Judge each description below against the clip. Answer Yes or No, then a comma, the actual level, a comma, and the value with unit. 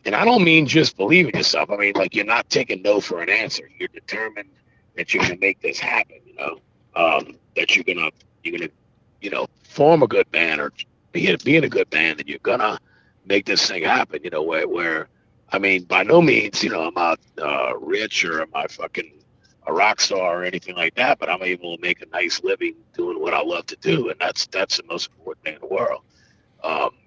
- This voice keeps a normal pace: No, fast, 230 wpm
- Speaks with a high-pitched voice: Yes, very high, 330 Hz